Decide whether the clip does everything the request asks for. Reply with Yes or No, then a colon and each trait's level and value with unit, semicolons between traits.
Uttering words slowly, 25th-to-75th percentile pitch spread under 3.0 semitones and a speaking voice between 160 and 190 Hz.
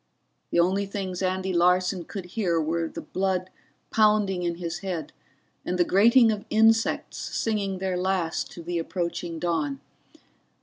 No: average, 145 wpm; narrow, 2.4 semitones; medium, 185 Hz